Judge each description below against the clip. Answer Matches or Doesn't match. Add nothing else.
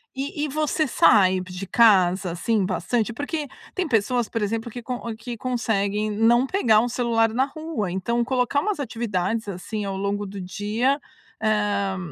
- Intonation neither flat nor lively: Matches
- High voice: Matches